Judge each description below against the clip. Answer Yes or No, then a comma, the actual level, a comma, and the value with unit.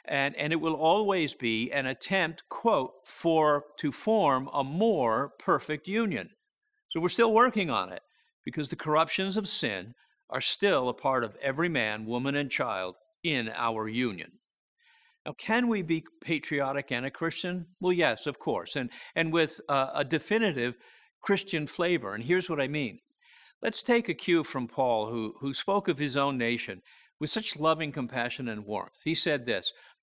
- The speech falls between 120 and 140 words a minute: No, average, 175 wpm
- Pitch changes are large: Yes, wide, 6.1 semitones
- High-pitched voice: No, medium, 155 Hz